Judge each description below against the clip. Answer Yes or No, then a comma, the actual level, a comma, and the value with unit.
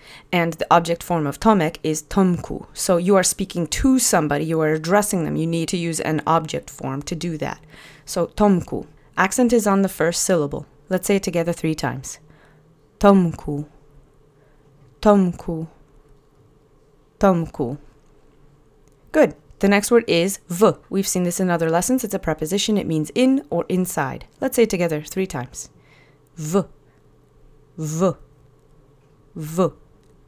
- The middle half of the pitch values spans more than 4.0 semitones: Yes, average, 4.6 semitones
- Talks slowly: No, average, 150 wpm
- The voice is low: No, medium, 165 Hz